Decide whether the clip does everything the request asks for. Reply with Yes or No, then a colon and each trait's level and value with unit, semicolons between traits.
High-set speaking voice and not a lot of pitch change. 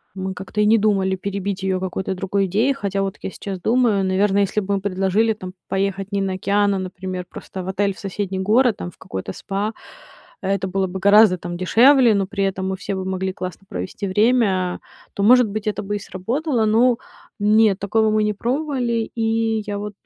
Yes: high, 200 Hz; narrow, 2.3 semitones